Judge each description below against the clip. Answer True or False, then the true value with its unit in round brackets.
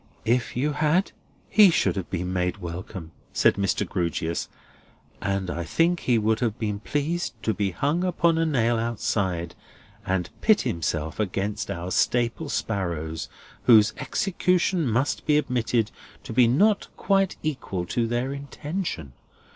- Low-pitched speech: True (115 Hz)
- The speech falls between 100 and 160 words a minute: True (145 wpm)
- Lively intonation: True (8.2 semitones)